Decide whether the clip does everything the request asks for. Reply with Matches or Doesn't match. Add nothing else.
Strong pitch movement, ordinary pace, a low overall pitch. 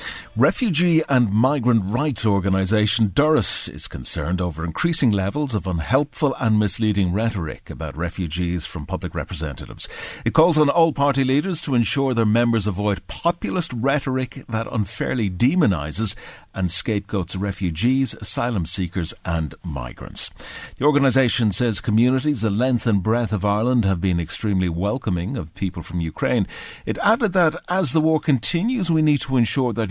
Matches